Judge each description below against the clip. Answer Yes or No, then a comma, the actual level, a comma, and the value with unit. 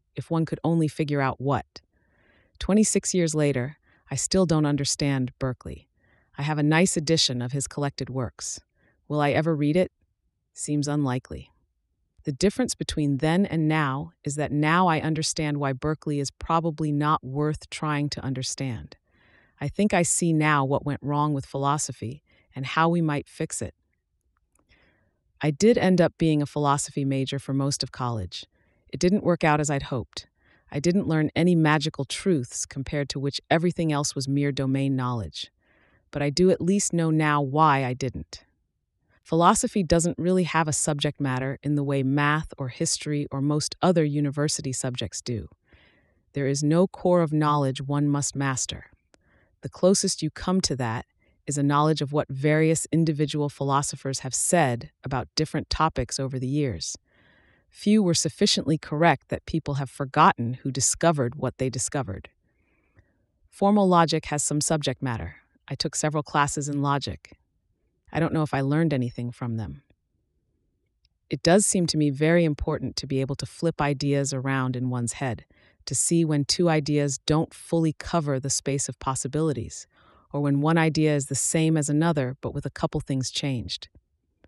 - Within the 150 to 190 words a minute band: Yes, average, 170 wpm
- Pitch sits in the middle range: Yes, medium, 145 Hz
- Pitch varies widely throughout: No, average, 3.2 semitones